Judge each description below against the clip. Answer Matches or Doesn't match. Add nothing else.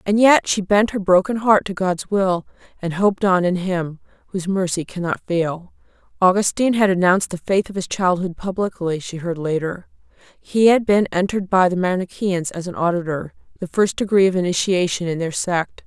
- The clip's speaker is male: Doesn't match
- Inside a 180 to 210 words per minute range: Matches